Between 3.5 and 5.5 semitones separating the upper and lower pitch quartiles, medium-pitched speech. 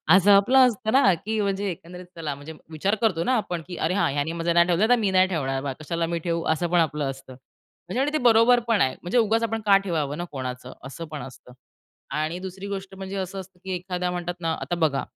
Yes: average, 4.0 semitones; medium, 180 Hz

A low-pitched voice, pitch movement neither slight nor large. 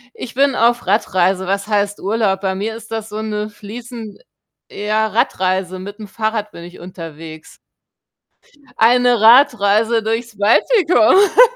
No: high, 215 Hz; average, 3.0 semitones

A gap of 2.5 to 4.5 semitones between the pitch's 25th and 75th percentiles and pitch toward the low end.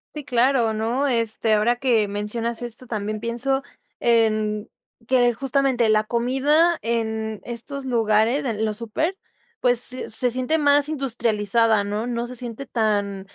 No: average, 2.9 semitones; high, 235 Hz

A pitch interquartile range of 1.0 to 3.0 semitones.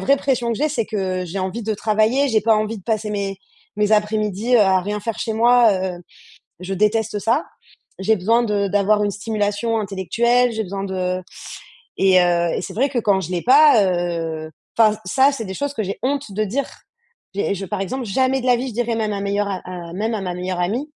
No: average, 3.4 semitones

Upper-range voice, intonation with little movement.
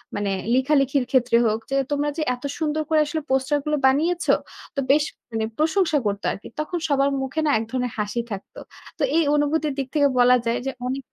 No: very high, 275 Hz; average, 3.4 semitones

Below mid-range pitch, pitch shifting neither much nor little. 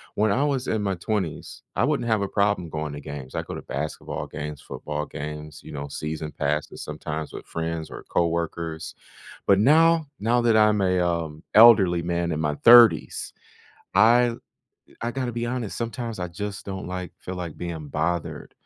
No: very low, 90 Hz; wide, 6.4 semitones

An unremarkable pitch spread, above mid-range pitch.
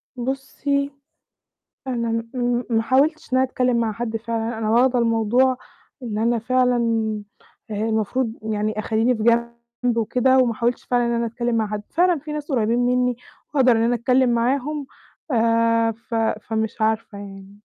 No: narrow, 2.2 semitones; high, 235 Hz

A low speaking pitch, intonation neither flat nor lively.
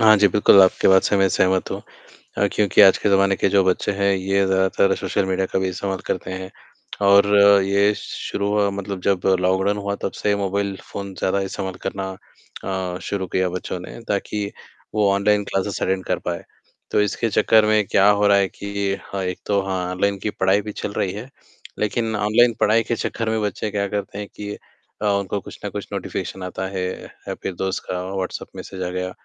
No: low, 100 Hz; narrow, 1.4 semitones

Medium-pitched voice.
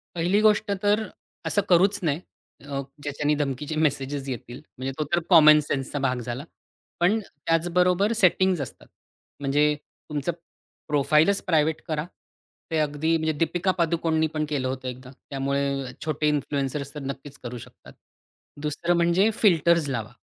Yes: medium, 150 Hz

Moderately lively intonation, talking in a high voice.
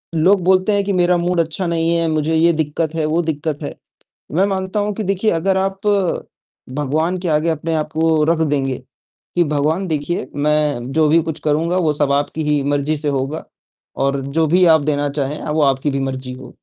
No: average, 3.0 semitones; medium, 155 Hz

